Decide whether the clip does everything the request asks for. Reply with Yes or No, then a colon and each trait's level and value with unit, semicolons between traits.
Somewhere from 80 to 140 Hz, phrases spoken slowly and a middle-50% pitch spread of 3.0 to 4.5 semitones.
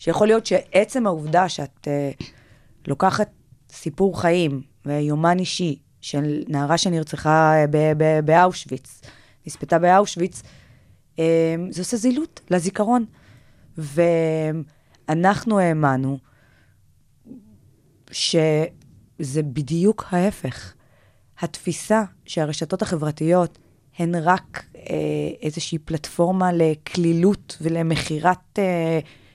No: medium, 160 Hz; slow, 80 wpm; average, 4.2 semitones